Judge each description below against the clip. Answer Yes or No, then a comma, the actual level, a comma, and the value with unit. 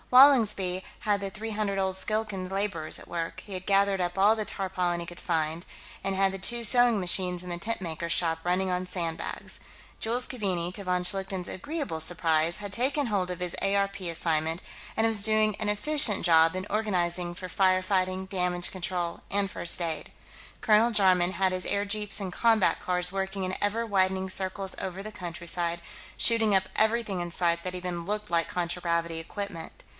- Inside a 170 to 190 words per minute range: Yes, average, 180 wpm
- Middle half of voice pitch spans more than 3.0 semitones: No, average, 2.7 semitones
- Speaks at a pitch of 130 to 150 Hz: No, high, 190 Hz